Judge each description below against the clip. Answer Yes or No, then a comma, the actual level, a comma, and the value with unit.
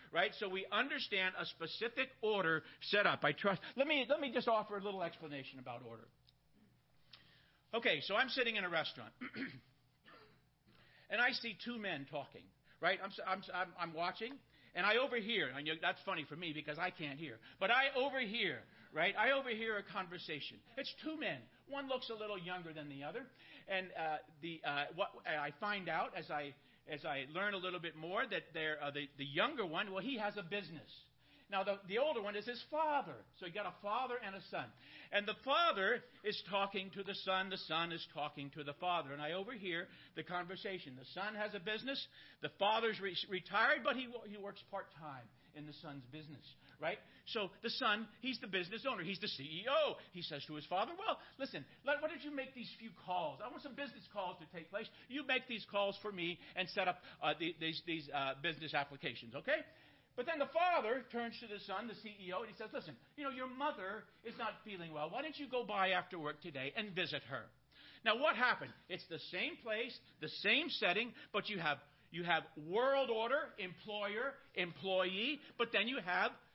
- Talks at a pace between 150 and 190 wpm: No, fast, 205 wpm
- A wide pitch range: Yes, wide, 6.3 semitones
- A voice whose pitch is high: Yes, high, 195 Hz